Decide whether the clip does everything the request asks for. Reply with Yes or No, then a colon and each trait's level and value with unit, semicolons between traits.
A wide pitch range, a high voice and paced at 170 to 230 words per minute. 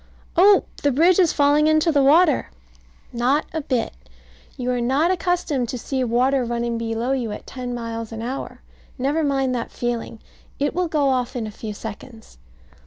No: average, 4.0 semitones; very high, 260 Hz; average, 175 wpm